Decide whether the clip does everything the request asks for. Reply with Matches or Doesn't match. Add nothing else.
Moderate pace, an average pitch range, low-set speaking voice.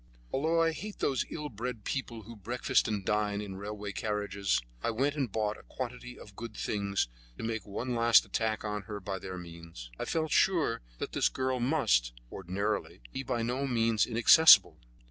Matches